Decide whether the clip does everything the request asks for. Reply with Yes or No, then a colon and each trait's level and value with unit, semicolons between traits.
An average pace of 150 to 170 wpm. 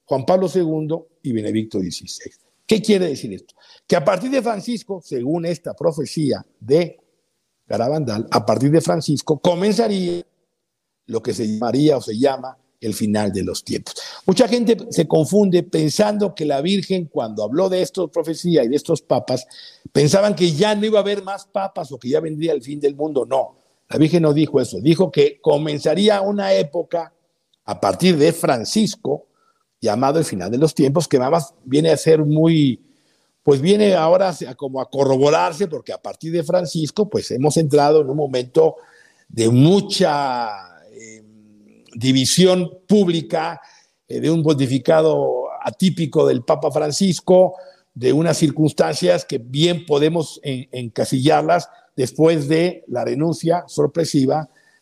Yes: average, 155 wpm